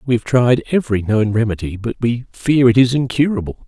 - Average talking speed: Yes, average, 195 wpm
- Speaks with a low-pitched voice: Yes, low, 120 Hz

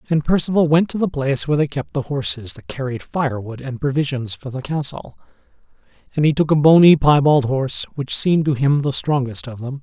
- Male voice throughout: Yes, male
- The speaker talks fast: Yes, fast, 210 wpm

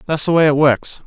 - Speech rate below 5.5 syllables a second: No, 5.7 syllables/s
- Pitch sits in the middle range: Yes, medium, 150 Hz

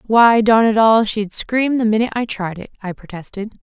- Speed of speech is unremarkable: No, fast, 215 wpm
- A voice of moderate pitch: No, high, 215 Hz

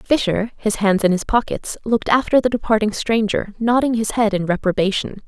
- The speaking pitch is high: Yes, high, 215 Hz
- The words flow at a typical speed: Yes, average, 180 wpm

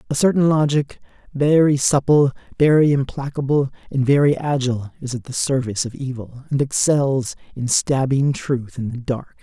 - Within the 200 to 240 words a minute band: No, average, 155 wpm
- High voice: No, low, 135 Hz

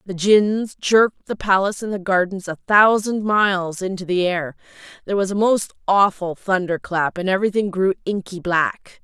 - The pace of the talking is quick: No, average, 175 wpm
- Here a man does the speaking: No, female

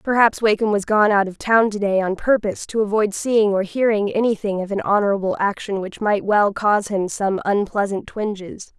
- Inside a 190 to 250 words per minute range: Yes, average, 200 wpm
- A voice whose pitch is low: No, high, 205 Hz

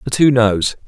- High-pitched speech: No, low, 120 Hz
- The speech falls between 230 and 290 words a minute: No, fast, 205 wpm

